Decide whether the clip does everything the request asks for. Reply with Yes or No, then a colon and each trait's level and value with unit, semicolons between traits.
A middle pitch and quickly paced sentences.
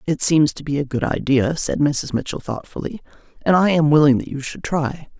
Yes: medium, 145 Hz; fast, 220 wpm